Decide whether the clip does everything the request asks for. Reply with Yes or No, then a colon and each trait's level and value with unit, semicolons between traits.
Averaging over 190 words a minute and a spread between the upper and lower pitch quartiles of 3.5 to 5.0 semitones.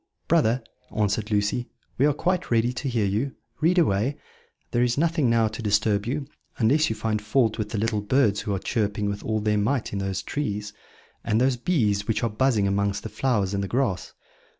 Yes: average, 200 wpm; average, 3.8 semitones